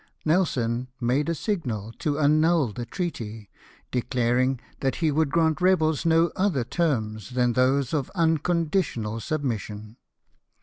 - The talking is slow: Yes, slow, 125 wpm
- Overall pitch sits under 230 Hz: Yes, medium, 140 Hz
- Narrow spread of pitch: No, wide, 5.4 semitones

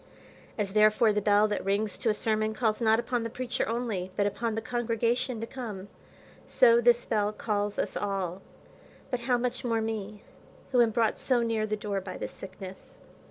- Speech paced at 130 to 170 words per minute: No, average, 190 wpm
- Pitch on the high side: Yes, high, 220 Hz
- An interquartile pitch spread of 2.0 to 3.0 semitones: Yes, narrow, 2.4 semitones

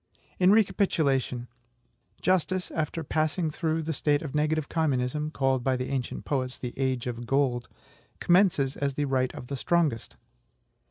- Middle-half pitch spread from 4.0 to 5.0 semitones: No, average, 3.6 semitones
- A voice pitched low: No, medium, 145 Hz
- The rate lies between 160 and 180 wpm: No, average, 150 wpm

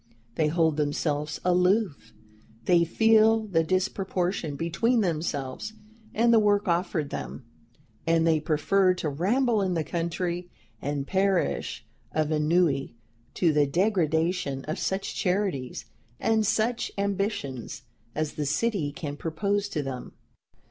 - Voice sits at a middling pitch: Yes, medium, 170 Hz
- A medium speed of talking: No, slow, 125 wpm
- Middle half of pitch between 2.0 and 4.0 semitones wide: No, average, 4.8 semitones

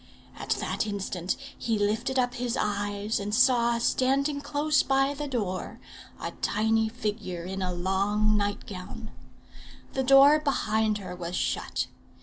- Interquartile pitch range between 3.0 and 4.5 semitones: Yes, average, 4.2 semitones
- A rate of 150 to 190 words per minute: No, average, 140 wpm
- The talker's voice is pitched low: No, high, 220 Hz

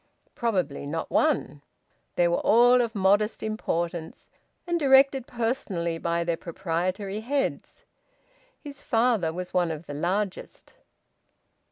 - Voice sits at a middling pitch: No, high, 195 Hz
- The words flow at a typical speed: No, slow, 120 wpm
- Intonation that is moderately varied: No, wide, 6.0 semitones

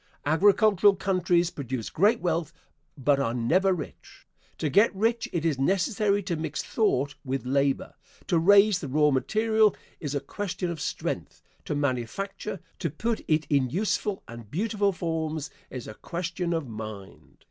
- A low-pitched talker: No, medium, 165 Hz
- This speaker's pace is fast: No, average, 155 wpm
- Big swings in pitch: Yes, wide, 6.0 semitones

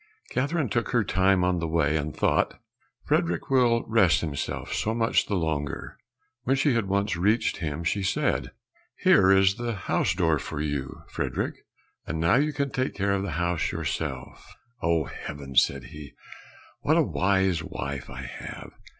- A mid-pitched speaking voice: No, very low, 90 Hz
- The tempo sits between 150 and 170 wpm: Yes, average, 165 wpm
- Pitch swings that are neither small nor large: No, wide, 6.0 semitones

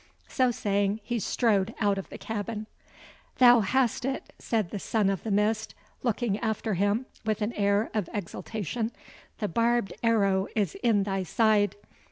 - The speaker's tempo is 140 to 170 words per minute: Yes, average, 160 wpm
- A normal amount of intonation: No, narrow, 2.3 semitones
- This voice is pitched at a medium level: No, high, 215 Hz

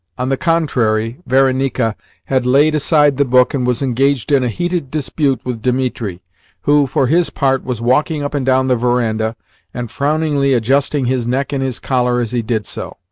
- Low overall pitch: Yes, low, 130 Hz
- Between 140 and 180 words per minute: No, average, 190 wpm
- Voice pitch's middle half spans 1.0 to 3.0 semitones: Yes, narrow, 2.6 semitones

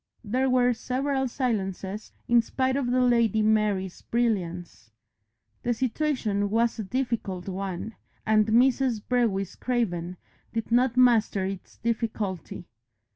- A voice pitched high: Yes, high, 225 Hz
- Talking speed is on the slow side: Yes, slow, 120 wpm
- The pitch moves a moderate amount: Yes, average, 4.0 semitones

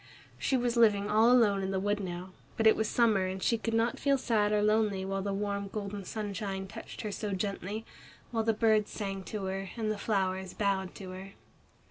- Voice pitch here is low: No, high, 205 Hz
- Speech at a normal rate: No, fast, 210 wpm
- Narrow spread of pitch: Yes, narrow, 2.3 semitones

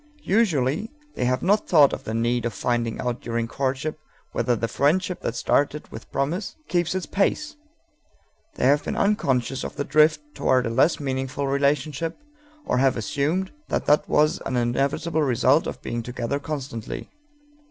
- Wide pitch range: No, average, 4.0 semitones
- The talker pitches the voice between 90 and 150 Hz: Yes, medium, 140 Hz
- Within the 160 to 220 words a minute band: Yes, average, 165 wpm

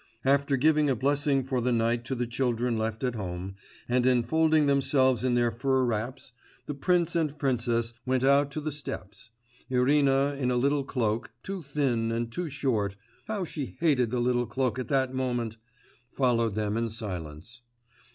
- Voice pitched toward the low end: Yes, low, 125 Hz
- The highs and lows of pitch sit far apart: No, average, 3.2 semitones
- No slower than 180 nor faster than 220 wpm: No, average, 170 wpm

